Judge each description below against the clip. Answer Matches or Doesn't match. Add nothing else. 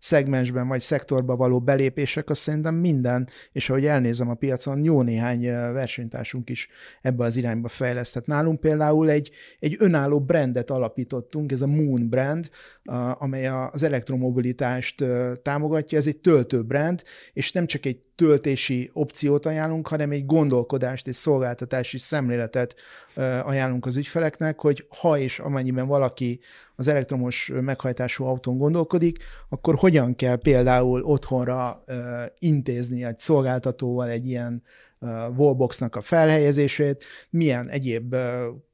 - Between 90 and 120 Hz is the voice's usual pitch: Doesn't match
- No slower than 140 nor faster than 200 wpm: Doesn't match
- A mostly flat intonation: Doesn't match